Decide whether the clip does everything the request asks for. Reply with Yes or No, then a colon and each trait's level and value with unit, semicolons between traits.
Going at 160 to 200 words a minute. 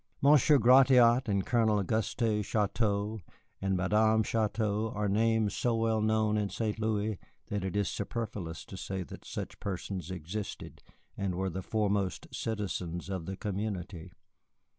No: average, 140 wpm